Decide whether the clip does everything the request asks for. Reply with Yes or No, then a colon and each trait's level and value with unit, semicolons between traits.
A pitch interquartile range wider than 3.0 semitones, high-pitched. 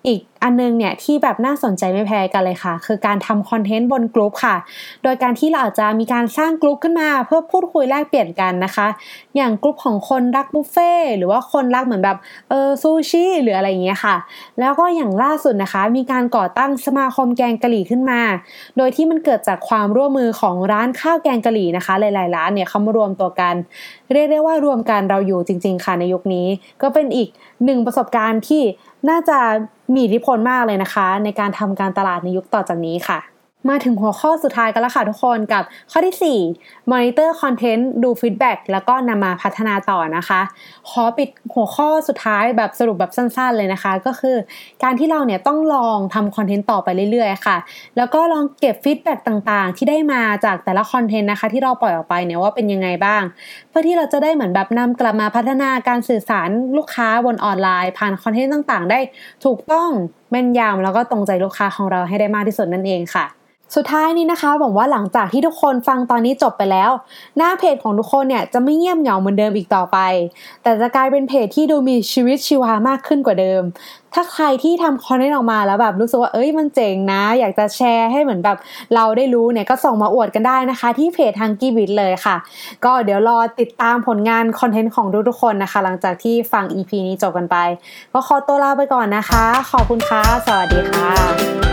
Yes: average, 5.0 semitones; high, 235 Hz